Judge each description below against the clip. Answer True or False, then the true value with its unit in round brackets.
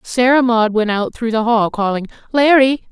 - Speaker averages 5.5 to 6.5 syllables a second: False (4.7 syllables/s)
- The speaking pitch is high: True (235 Hz)